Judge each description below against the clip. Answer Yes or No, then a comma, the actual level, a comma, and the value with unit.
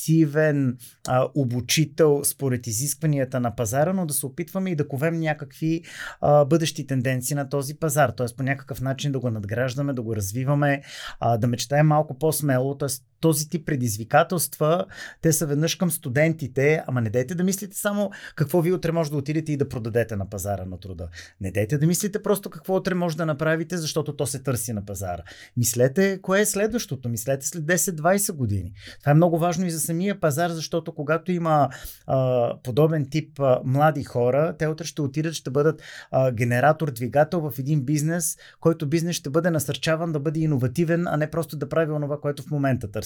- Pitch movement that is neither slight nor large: Yes, average, 4.0 semitones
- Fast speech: Yes, fast, 185 wpm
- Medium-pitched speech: Yes, medium, 150 Hz